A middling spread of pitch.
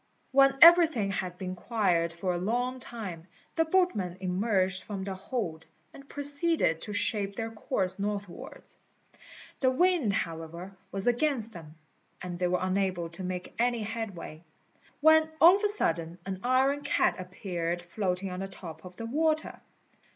No: wide, 6.1 semitones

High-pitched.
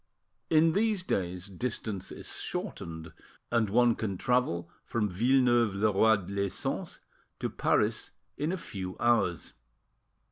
No: low, 110 Hz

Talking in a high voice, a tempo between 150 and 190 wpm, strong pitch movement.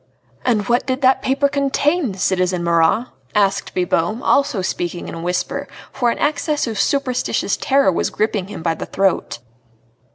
Yes: high, 220 Hz; average, 160 wpm; wide, 7.0 semitones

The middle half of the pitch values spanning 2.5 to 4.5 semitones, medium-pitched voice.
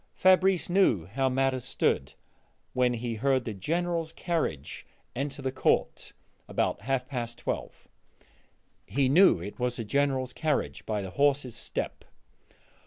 No: average, 3.5 semitones; low, 130 Hz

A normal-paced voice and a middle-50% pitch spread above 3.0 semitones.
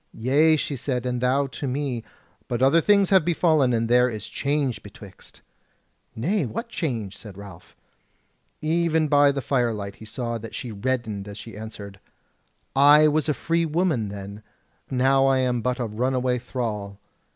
Yes: average, 160 wpm; average, 4.8 semitones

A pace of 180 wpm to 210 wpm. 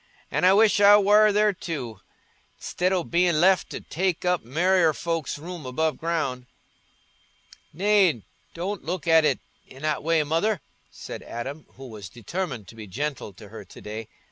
No: average, 170 wpm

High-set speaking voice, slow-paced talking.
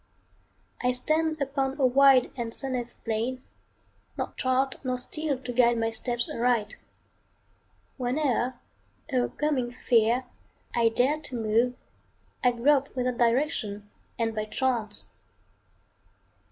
Yes: very high, 250 Hz; slow, 115 wpm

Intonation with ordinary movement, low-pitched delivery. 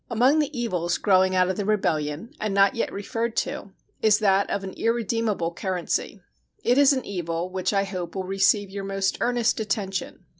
No: average, 3.4 semitones; high, 195 Hz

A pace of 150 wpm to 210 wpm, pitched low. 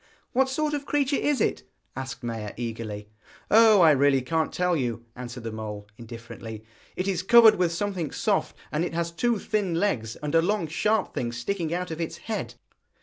No: average, 190 wpm; medium, 165 Hz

